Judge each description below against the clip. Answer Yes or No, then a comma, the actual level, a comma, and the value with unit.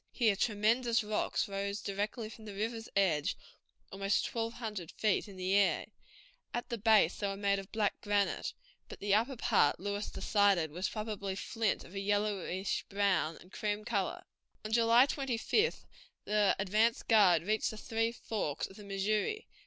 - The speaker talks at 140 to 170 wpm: Yes, average, 165 wpm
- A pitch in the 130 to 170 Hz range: No, high, 205 Hz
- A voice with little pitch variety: Yes, narrow, 2.3 semitones